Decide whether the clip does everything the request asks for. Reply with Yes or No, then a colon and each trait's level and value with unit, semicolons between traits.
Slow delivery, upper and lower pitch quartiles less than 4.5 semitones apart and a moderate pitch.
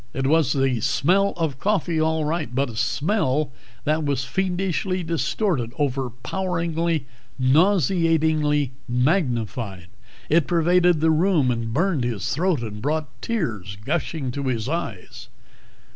No: slow, 125 wpm; average, 5.2 semitones; medium, 150 Hz